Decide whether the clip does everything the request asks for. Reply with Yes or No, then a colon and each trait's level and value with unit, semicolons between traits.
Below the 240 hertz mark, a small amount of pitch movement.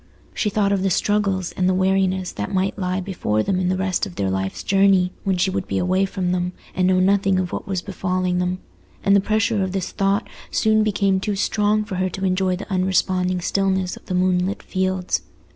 Yes: high, 190 Hz; narrow, 1.3 semitones